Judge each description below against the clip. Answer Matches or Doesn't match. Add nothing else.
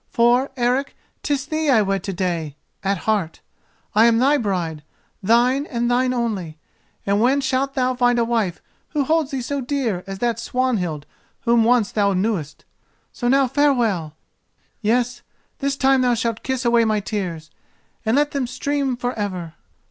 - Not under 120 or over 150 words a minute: Doesn't match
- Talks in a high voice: Matches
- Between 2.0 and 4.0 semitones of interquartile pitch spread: Doesn't match